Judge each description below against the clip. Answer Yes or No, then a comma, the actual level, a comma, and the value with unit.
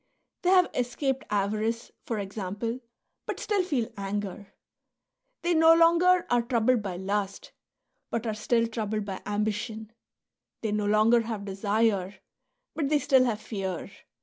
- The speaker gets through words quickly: No, average, 140 wpm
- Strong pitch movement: No, average, 3.6 semitones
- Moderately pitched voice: No, high, 220 Hz